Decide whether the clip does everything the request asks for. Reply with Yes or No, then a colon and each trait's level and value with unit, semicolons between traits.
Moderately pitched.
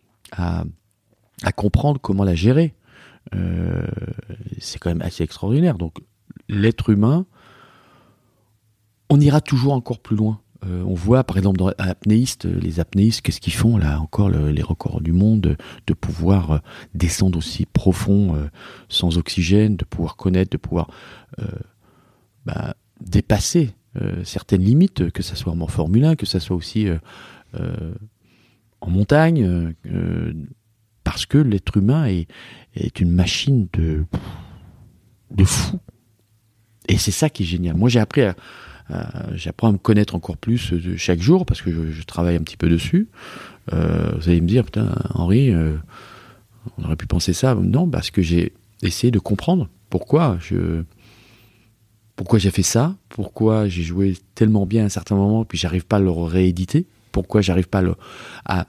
No: low, 105 Hz